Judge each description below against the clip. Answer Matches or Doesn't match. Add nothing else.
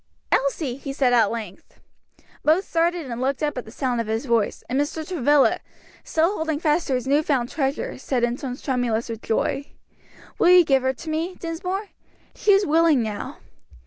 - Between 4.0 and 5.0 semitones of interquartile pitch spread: Matches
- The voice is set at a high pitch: Matches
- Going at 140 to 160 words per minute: Doesn't match